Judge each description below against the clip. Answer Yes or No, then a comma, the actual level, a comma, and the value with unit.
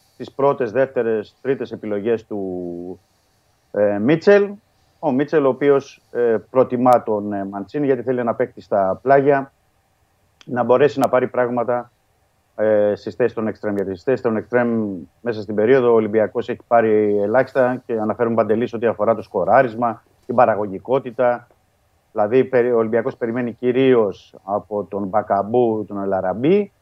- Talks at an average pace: Yes, average, 145 wpm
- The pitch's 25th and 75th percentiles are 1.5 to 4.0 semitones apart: Yes, average, 3.5 semitones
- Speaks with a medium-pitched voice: No, low, 115 Hz